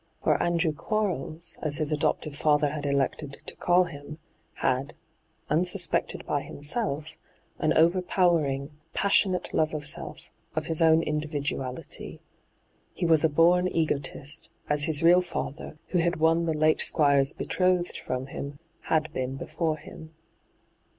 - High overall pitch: No, medium, 155 Hz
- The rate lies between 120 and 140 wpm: Yes, slow, 135 wpm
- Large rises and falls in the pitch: No, average, 2.9 semitones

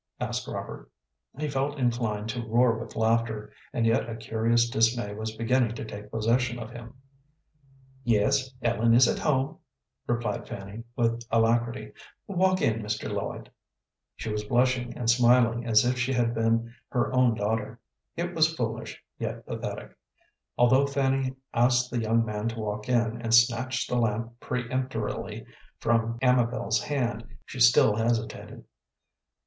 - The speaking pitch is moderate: No, low, 115 Hz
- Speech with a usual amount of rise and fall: No, narrow, 1.9 semitones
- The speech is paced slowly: No, average, 145 wpm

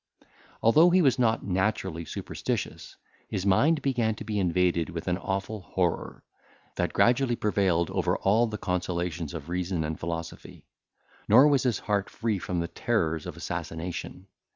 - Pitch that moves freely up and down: No, average, 4.9 semitones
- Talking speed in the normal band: Yes, average, 155 wpm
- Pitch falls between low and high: No, very low, 95 Hz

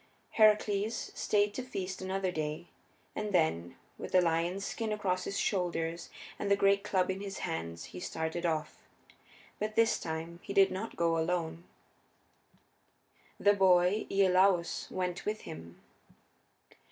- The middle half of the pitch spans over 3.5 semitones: No, average, 3.2 semitones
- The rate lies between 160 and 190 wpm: No, average, 140 wpm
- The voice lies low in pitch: No, medium, 185 Hz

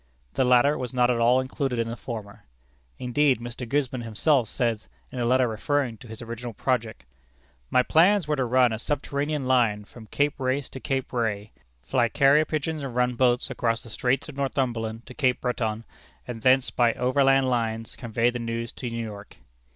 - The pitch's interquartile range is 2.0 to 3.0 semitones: Yes, narrow, 2.6 semitones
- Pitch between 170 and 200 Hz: No, low, 125 Hz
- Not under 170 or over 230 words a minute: Yes, average, 190 wpm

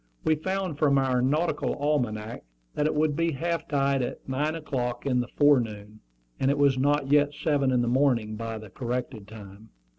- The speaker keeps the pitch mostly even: No, average, 3.6 semitones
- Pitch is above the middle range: No, low, 135 Hz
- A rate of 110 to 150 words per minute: No, average, 185 wpm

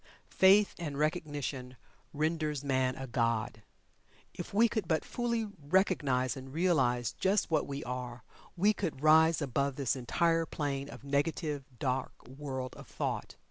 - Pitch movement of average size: Yes, average, 4.2 semitones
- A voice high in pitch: No, medium, 145 Hz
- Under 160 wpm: Yes, average, 140 wpm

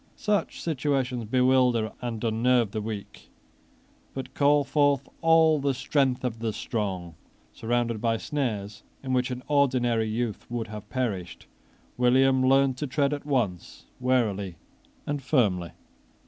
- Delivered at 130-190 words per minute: Yes, slow, 135 wpm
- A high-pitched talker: No, low, 125 Hz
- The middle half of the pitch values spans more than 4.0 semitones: No, average, 3.6 semitones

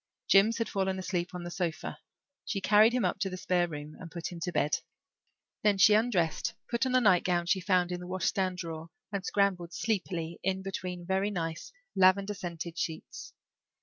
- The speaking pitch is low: No, medium, 185 Hz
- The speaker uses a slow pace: No, average, 185 wpm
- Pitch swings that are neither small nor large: No, narrow, 2.3 semitones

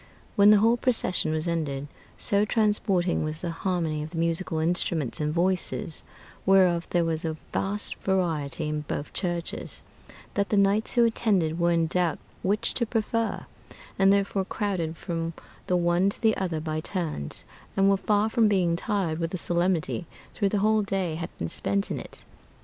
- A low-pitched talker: No, medium, 175 Hz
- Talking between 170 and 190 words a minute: Yes, average, 175 wpm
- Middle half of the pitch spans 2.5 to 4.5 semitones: Yes, average, 3.6 semitones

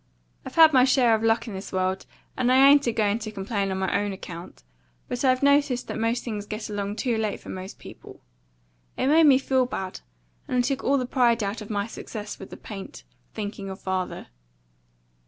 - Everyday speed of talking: No, fast, 210 wpm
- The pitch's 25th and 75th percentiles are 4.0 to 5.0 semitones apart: Yes, average, 4.3 semitones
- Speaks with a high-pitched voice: Yes, high, 220 Hz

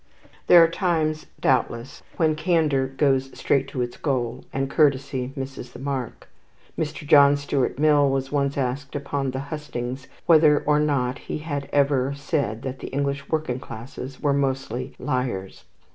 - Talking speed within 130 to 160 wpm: Yes, average, 155 wpm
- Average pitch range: No, narrow, 2.2 semitones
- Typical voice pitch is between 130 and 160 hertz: Yes, medium, 140 Hz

